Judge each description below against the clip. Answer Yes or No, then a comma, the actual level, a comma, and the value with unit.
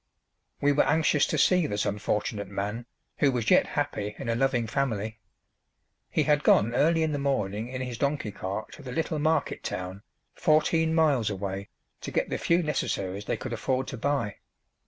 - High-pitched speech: No, low, 125 Hz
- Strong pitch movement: Yes, wide, 6.1 semitones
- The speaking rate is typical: Yes, average, 180 wpm